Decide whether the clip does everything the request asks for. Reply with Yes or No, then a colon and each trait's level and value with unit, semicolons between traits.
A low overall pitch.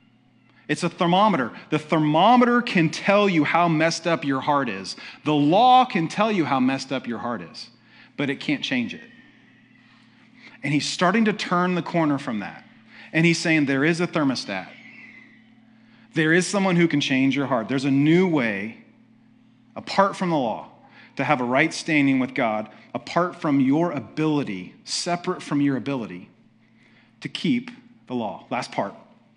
No: medium, 170 Hz